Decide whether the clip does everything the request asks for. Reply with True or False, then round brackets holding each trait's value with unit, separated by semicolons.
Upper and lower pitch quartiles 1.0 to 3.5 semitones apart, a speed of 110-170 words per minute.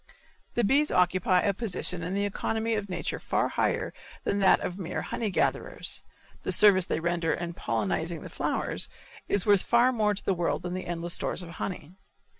False (3.0 semitones; 185 wpm)